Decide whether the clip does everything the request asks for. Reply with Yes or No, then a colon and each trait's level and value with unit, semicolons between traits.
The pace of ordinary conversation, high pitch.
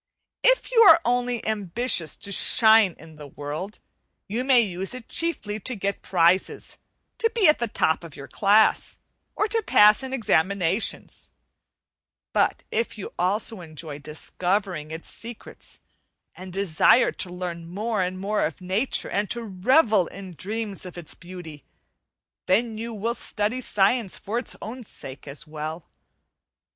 Yes: average, 150 wpm; high, 200 Hz